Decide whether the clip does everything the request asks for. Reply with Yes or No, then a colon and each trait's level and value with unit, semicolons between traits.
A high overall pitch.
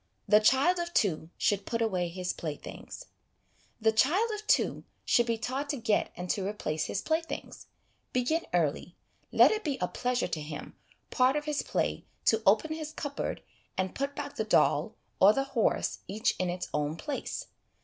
Yes: high, 230 Hz